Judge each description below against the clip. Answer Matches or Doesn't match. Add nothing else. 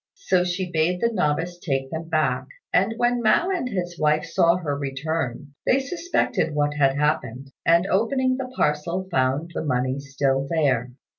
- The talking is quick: Doesn't match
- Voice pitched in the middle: Matches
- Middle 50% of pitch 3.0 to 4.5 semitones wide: Doesn't match